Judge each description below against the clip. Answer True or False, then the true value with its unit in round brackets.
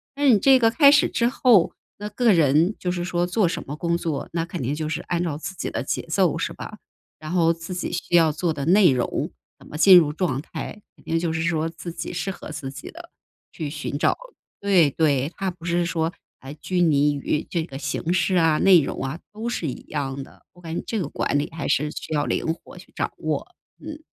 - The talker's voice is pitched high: False (170 Hz)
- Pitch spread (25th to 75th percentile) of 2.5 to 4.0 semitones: True (3.4 semitones)